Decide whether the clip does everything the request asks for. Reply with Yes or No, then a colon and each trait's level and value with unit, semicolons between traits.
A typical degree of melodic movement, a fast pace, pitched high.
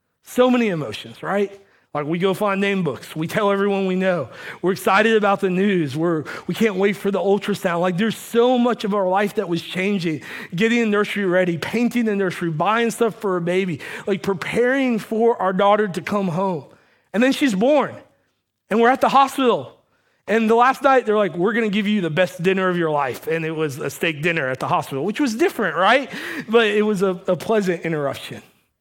Yes: average, 3.9 semitones; fast, 220 wpm; high, 200 Hz